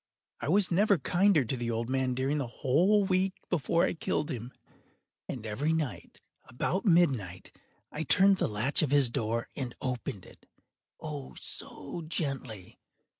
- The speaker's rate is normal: Yes, average, 155 wpm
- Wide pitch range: Yes, wide, 6.4 semitones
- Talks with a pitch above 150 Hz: No, medium, 140 Hz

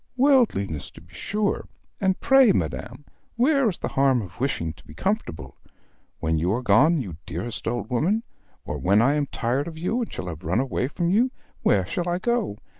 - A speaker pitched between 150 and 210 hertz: No, medium, 140 Hz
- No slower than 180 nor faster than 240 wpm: Yes, average, 190 wpm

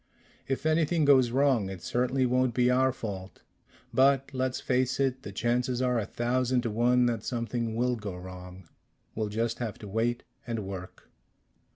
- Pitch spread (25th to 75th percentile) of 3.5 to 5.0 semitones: No, average, 2.9 semitones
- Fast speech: No, average, 170 wpm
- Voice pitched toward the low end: Yes, low, 120 Hz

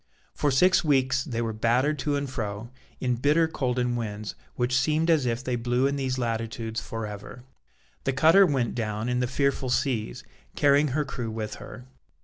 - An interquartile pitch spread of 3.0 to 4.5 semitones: Yes, average, 3.5 semitones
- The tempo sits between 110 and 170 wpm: No, average, 185 wpm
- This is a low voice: Yes, low, 125 Hz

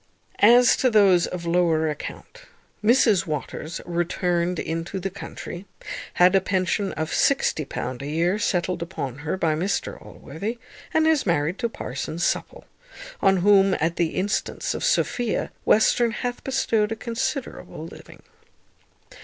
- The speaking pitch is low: No, medium, 185 Hz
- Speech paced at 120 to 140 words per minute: Yes, slow, 135 wpm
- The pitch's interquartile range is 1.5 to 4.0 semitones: No, average, 4.7 semitones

